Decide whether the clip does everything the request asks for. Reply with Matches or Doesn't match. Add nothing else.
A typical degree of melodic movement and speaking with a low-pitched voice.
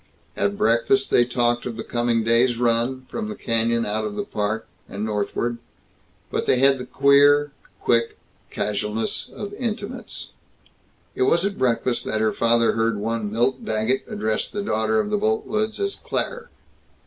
Matches